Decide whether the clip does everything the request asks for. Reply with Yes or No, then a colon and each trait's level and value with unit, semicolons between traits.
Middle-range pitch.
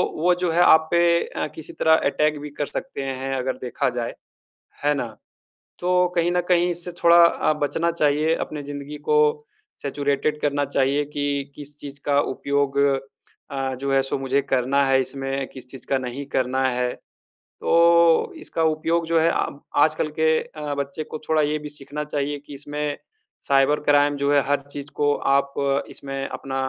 Yes: medium, 145 Hz